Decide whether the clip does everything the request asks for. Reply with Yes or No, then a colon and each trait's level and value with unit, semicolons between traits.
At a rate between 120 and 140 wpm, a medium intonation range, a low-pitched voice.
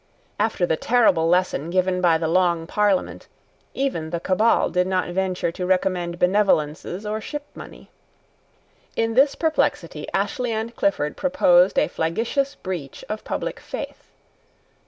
No: slow, 135 wpm; average, 4.4 semitones; medium, 185 Hz